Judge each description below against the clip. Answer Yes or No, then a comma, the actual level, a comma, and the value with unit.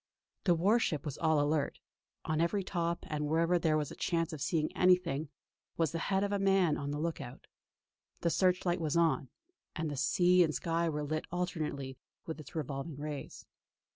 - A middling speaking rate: Yes, average, 190 wpm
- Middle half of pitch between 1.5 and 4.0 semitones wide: Yes, average, 2.9 semitones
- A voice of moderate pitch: Yes, medium, 160 Hz